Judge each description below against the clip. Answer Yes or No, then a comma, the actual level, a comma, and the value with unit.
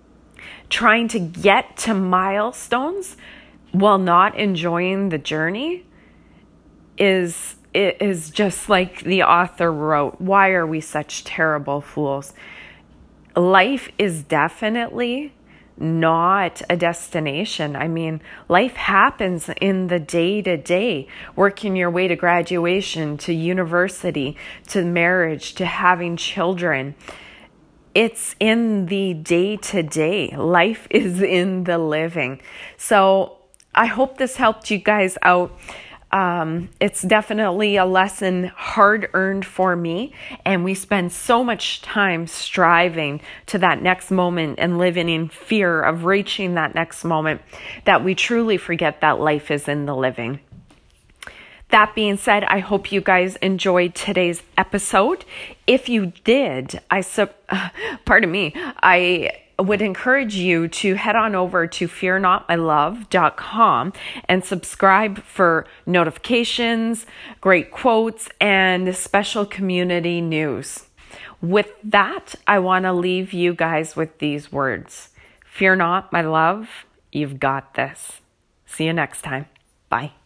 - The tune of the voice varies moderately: Yes, average, 3.4 semitones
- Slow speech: Yes, slow, 125 wpm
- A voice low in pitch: No, medium, 185 Hz